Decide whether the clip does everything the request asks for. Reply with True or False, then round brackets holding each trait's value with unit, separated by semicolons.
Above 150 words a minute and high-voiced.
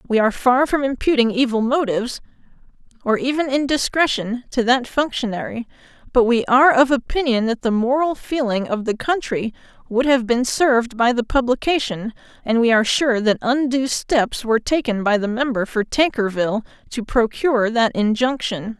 True (160 wpm; 245 Hz)